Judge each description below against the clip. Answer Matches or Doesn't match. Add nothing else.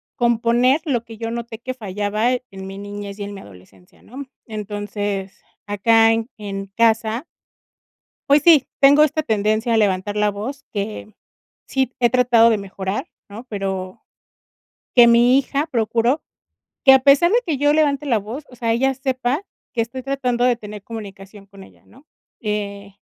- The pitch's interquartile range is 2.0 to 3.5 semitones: Doesn't match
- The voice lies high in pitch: Matches